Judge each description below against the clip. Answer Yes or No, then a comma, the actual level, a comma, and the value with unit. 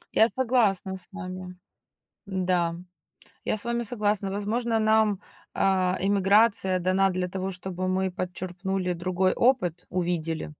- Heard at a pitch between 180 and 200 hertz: Yes, high, 190 Hz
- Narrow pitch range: Yes, narrow, 2.3 semitones